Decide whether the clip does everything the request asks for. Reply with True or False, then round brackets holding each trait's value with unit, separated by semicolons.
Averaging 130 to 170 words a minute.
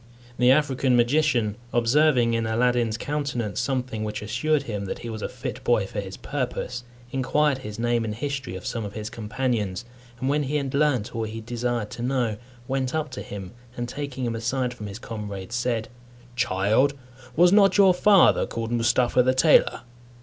False (180 wpm)